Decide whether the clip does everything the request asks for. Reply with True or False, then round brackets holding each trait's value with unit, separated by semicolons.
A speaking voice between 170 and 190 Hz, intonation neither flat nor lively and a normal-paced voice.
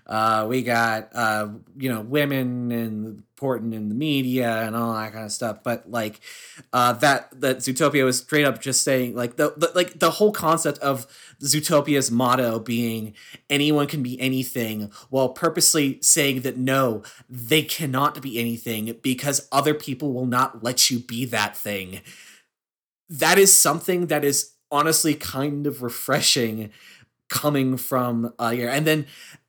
False (130 Hz; 3.8 semitones; 155 wpm)